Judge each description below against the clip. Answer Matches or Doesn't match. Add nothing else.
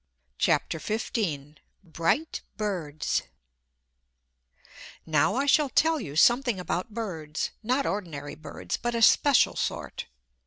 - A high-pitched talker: Matches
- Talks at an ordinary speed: Doesn't match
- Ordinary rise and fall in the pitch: Doesn't match